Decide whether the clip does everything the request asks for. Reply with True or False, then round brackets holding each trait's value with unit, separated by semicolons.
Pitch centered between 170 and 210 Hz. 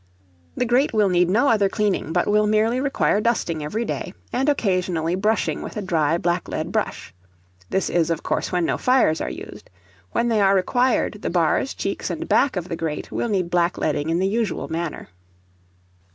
True (190 Hz)